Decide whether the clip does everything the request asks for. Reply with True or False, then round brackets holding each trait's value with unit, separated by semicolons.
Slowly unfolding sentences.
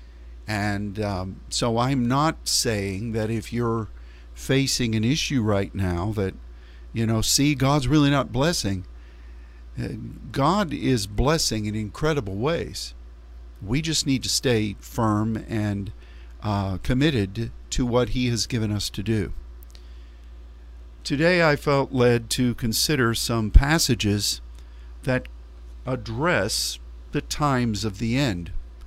True (125 wpm)